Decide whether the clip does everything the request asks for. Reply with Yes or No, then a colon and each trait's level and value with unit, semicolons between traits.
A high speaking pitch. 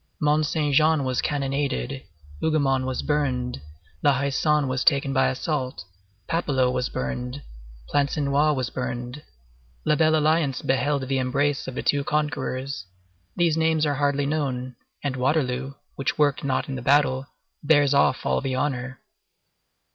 No: medium, 140 Hz